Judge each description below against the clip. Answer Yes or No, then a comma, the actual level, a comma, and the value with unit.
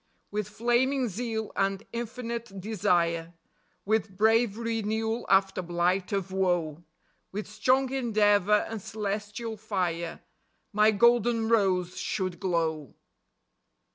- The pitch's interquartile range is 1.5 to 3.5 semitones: Yes, average, 3.2 semitones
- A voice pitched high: Yes, high, 210 Hz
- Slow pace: Yes, slow, 105 wpm